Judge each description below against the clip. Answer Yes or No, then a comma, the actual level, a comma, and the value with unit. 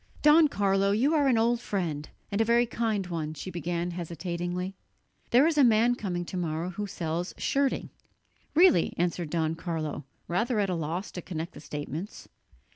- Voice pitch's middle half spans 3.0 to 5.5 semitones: Yes, average, 5.1 semitones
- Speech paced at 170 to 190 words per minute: Yes, average, 175 wpm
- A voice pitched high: No, medium, 180 Hz